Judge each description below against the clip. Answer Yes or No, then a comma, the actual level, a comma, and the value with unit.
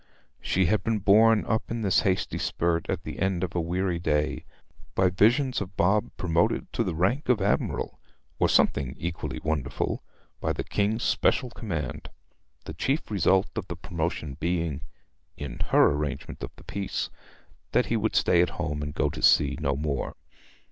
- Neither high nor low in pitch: No, very low, 90 Hz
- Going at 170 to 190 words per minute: Yes, average, 175 wpm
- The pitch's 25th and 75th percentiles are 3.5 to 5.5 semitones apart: Yes, average, 4.9 semitones